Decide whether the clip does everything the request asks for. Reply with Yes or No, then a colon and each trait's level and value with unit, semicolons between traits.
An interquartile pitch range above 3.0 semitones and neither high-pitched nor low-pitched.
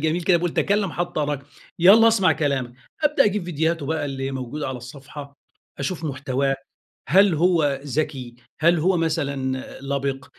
Yes: average, 4.1 semitones; medium, 150 Hz